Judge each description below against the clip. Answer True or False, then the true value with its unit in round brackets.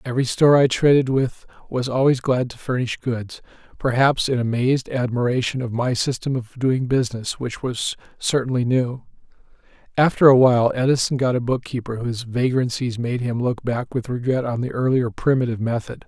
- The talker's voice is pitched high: False (125 Hz)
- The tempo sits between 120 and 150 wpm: False (170 wpm)